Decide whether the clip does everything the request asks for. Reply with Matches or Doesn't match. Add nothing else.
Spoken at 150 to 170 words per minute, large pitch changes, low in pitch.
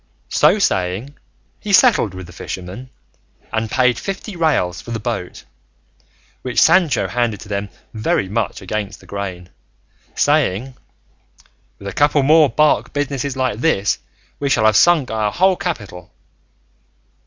Doesn't match